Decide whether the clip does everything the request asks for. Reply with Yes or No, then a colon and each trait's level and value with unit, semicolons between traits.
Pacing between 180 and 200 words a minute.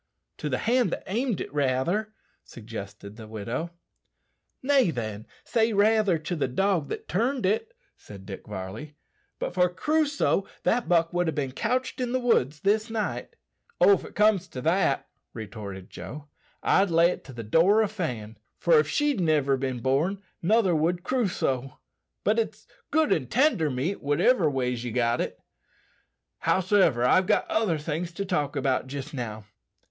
No: average, 165 wpm